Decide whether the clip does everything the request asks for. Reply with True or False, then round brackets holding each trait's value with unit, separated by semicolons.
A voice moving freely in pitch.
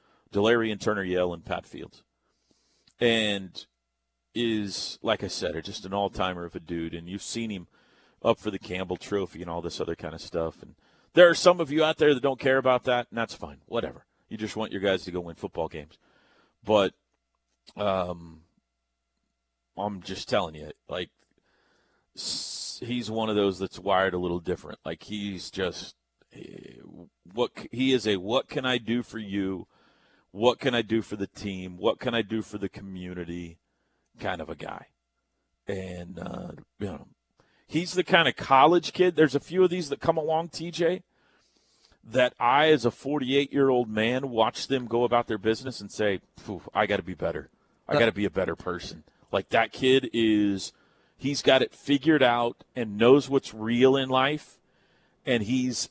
True (5.9 semitones)